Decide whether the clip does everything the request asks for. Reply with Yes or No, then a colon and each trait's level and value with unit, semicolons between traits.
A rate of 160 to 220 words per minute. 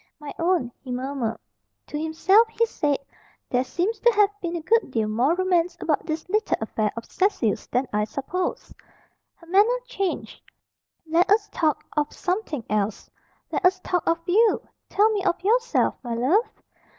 Yes: average, 165 wpm